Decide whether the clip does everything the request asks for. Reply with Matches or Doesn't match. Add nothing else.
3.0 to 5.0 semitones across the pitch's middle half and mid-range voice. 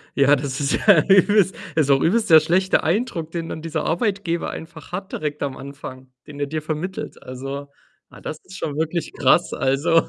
Matches